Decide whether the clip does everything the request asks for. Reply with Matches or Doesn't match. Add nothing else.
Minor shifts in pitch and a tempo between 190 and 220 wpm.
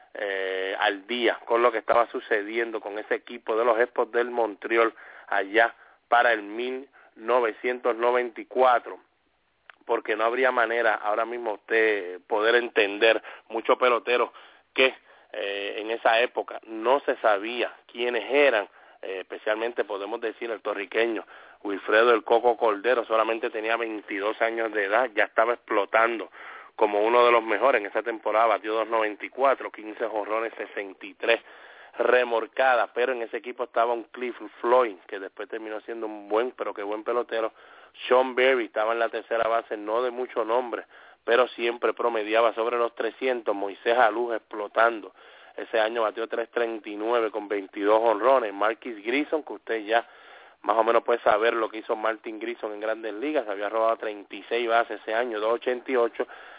Doesn't match